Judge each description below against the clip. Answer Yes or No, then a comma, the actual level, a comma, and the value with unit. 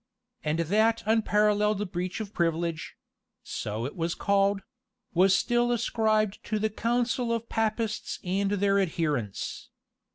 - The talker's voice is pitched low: No, high, 205 Hz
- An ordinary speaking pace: No, slow, 125 wpm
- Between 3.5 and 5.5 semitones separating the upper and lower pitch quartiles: Yes, average, 3.8 semitones